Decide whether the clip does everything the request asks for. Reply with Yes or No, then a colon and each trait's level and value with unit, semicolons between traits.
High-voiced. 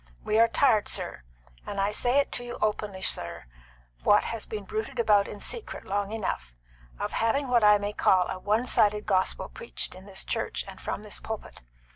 Yes: high, 210 Hz